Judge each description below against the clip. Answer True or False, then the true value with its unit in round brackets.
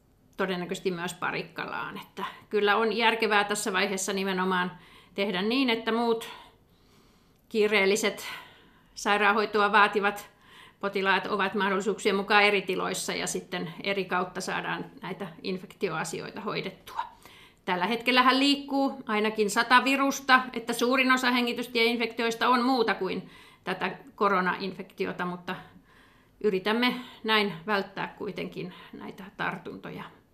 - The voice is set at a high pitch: True (210 Hz)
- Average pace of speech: True (105 wpm)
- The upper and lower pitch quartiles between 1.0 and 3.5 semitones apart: True (3.2 semitones)